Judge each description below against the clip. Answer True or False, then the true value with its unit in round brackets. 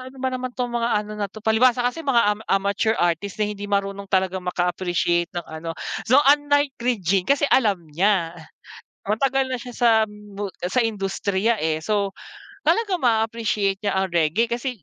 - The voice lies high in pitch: True (210 Hz)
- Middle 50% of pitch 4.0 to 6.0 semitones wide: True (4.3 semitones)